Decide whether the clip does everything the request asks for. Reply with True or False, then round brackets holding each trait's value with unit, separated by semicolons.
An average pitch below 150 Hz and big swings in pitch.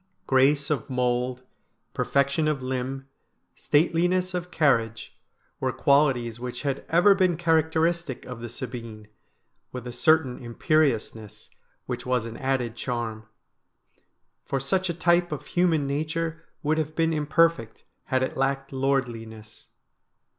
False (135 Hz; 4.6 semitones)